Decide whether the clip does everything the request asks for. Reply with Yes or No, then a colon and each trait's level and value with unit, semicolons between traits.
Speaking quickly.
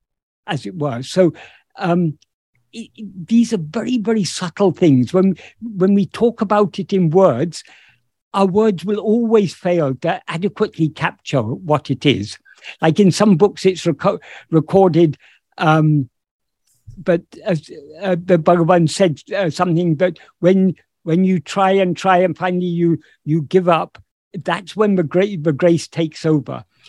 No: average, 155 wpm